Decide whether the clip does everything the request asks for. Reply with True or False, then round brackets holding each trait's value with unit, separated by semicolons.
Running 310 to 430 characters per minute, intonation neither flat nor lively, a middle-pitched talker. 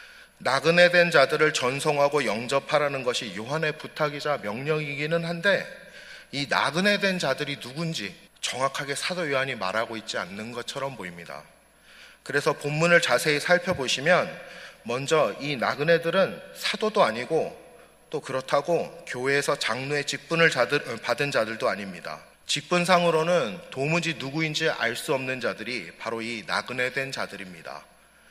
True (320 characters per minute; 4.5 semitones; 145 Hz)